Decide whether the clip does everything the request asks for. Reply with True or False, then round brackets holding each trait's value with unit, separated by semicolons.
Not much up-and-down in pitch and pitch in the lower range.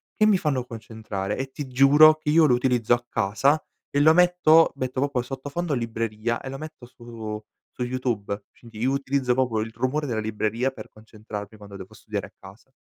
False (4.1 semitones; 125 Hz)